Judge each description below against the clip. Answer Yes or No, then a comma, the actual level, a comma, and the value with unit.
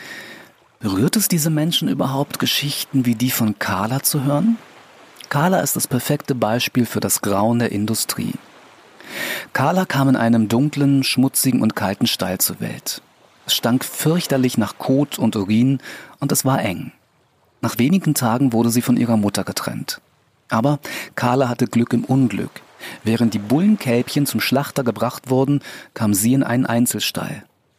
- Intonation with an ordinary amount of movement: Yes, average, 3.4 semitones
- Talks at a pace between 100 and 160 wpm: Yes, average, 155 wpm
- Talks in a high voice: No, low, 125 Hz